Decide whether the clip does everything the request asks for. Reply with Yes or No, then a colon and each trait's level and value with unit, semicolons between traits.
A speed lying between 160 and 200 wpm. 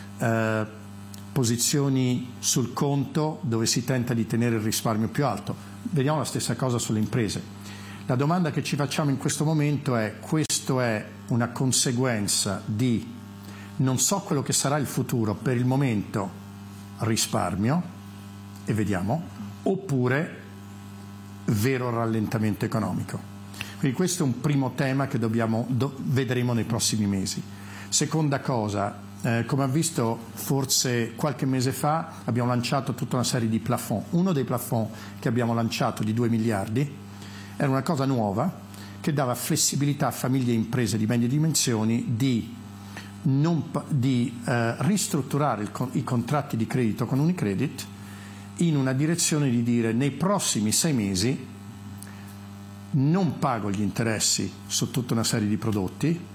No: average, 145 wpm